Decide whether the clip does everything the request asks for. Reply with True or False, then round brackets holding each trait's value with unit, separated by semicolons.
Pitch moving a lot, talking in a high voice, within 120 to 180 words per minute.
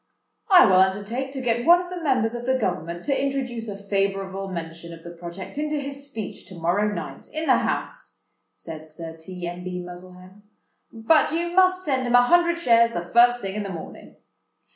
False (7.2 semitones; 210 Hz; 200 wpm)